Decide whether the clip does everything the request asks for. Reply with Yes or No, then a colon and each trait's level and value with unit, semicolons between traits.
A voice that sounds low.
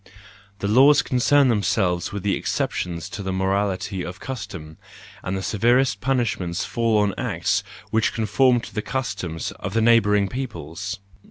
Yes: low, 105 Hz